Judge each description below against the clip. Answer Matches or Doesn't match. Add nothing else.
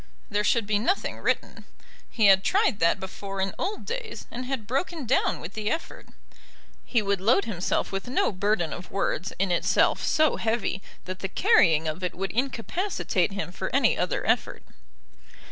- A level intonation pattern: Doesn't match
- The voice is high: Matches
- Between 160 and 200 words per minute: Matches